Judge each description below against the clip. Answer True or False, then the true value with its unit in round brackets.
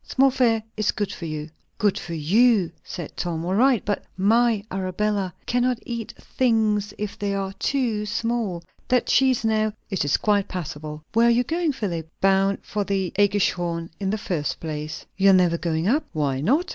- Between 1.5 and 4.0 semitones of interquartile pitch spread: False (4.7 semitones)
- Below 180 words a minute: False (185 wpm)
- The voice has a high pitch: True (200 Hz)